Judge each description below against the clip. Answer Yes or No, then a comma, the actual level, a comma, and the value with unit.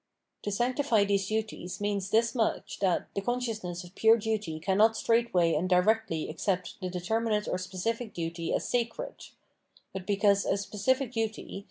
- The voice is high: Yes, high, 205 Hz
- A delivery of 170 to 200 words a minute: No, average, 155 wpm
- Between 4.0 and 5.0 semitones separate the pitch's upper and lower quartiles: No, average, 3.6 semitones